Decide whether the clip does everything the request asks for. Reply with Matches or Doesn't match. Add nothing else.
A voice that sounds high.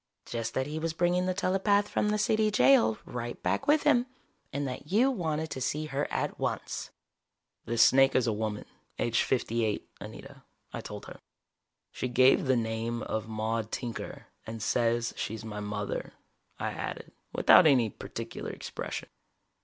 Doesn't match